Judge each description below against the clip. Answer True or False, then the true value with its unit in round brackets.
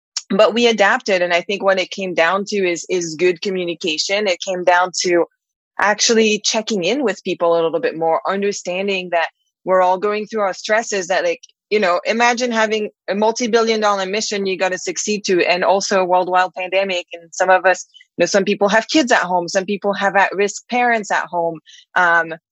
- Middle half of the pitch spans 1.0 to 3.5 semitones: True (2.9 semitones)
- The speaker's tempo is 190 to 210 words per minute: True (205 wpm)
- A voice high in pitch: True (195 Hz)